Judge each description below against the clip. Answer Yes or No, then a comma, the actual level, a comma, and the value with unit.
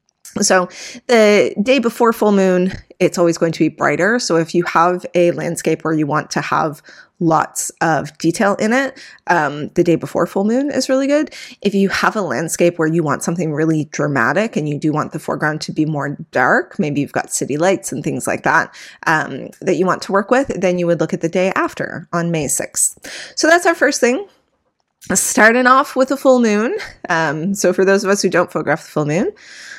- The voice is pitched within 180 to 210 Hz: Yes, medium, 185 Hz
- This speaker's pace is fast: Yes, fast, 220 wpm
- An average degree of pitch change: No, wide, 6.2 semitones